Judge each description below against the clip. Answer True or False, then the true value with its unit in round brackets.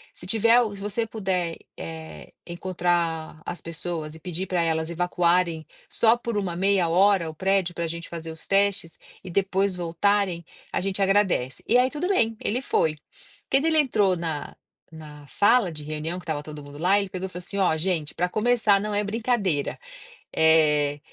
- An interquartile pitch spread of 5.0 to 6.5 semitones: False (3.8 semitones)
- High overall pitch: False (180 Hz)